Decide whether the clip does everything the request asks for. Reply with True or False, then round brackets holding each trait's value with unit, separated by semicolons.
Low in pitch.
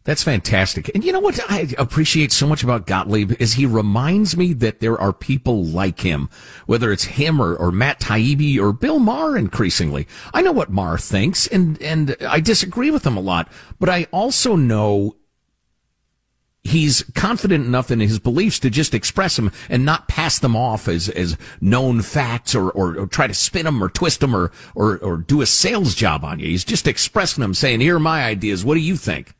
True (125 Hz)